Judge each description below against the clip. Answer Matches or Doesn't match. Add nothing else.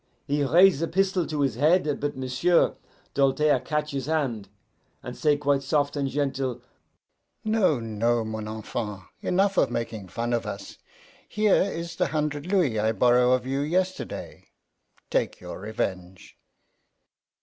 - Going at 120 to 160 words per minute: Matches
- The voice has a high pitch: Doesn't match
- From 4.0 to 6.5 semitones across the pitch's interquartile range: Matches